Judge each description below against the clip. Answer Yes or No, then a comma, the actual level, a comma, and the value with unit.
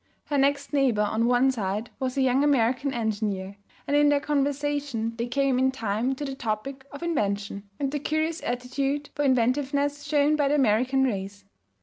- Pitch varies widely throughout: No, average, 3.9 semitones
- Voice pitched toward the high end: Yes, very high, 265 Hz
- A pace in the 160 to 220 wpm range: Yes, average, 180 wpm